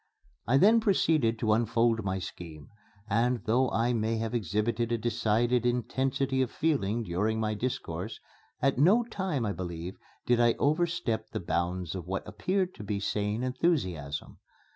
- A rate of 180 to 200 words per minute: No, average, 155 wpm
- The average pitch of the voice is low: Yes, low, 115 Hz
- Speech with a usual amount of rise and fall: Yes, average, 4.1 semitones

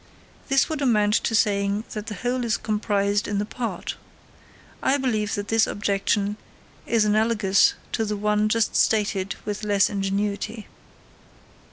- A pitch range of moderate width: No, narrow, 1.7 semitones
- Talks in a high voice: Yes, high, 210 Hz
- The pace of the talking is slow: No, average, 145 wpm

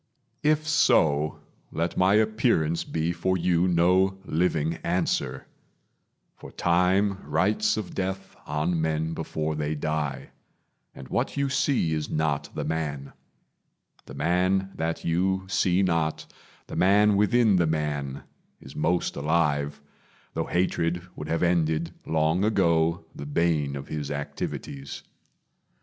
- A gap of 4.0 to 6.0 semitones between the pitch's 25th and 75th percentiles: No, average, 3.5 semitones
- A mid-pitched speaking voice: No, very low, 85 Hz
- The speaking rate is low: Yes, slow, 130 wpm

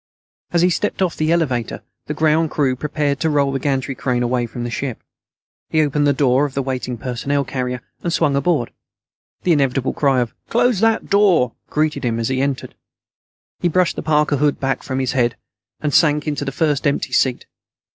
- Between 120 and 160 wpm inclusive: No, average, 195 wpm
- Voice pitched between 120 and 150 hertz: Yes, medium, 140 Hz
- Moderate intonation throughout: Yes, average, 3.3 semitones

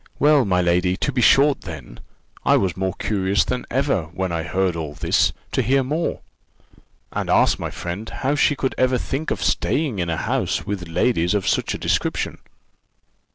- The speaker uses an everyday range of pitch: No, wide, 7.1 semitones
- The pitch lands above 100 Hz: No, very low, 95 Hz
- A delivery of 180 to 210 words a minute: Yes, average, 185 wpm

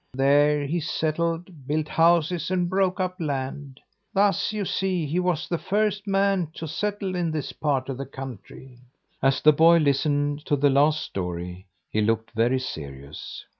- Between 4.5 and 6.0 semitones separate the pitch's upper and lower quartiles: Yes, average, 4.9 semitones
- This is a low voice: No, medium, 150 Hz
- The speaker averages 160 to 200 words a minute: Yes, average, 165 wpm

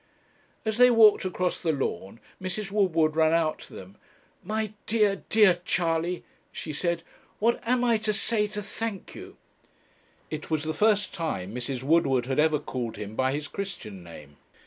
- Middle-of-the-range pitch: Yes, medium, 170 Hz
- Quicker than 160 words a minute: Yes, average, 170 wpm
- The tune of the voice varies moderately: No, wide, 7.2 semitones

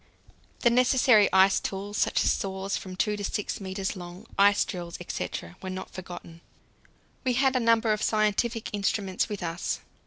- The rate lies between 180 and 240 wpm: No, average, 165 wpm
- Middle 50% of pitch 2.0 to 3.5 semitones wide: Yes, average, 2.9 semitones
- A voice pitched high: Yes, high, 200 Hz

